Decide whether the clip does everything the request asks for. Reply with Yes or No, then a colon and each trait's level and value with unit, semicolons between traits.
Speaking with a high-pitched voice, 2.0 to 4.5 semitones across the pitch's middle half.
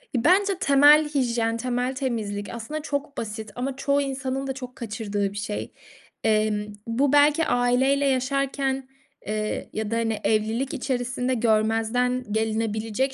Yes: high, 245 Hz; average, 3.7 semitones